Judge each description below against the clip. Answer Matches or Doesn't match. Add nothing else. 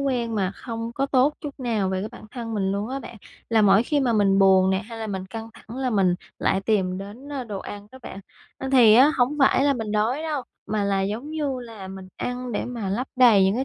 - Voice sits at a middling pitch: Doesn't match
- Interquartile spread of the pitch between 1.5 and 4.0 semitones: Doesn't match